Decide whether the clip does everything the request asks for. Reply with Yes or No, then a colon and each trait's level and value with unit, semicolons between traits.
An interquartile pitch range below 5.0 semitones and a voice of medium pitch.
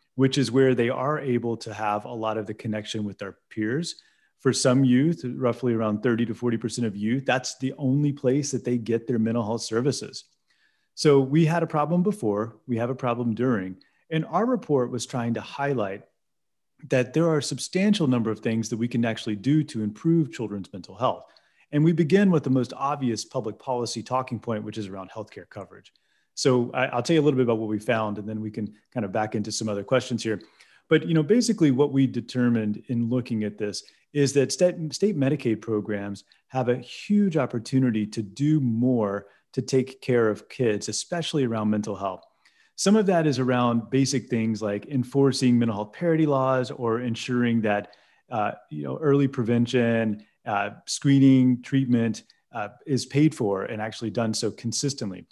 No: average, 3.8 semitones; low, 120 Hz